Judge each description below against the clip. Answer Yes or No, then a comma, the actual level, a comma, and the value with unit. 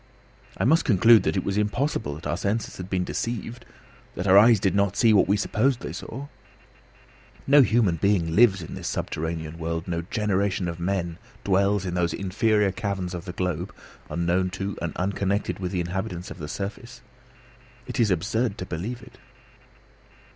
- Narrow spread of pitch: No, average, 3.7 semitones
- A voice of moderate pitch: No, very low, 95 Hz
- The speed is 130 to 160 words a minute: No, average, 175 wpm